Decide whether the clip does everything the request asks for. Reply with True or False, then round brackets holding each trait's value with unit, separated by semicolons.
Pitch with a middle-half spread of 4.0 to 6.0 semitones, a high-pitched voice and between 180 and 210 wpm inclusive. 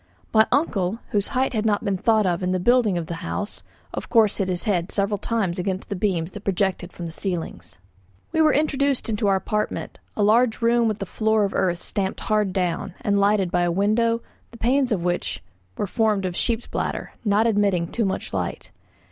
False (3.5 semitones; 205 Hz; 200 wpm)